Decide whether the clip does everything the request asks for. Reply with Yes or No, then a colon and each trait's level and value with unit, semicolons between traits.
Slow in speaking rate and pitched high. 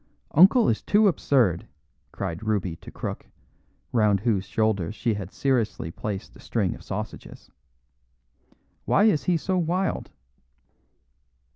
No: slow, 125 wpm; low, 110 Hz